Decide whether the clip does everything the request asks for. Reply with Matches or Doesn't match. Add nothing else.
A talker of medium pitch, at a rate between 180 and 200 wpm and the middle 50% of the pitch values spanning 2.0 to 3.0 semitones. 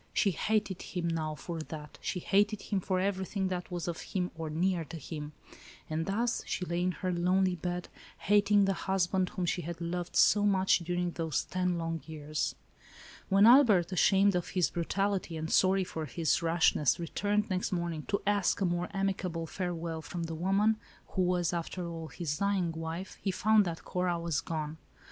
Matches